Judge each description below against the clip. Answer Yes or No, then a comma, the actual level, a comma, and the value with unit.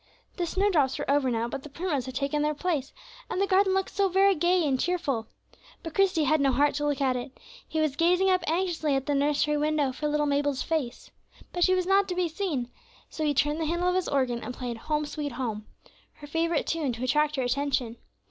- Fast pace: Yes, fast, 225 wpm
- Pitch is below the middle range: No, very high, 300 Hz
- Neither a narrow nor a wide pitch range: Yes, average, 4.4 semitones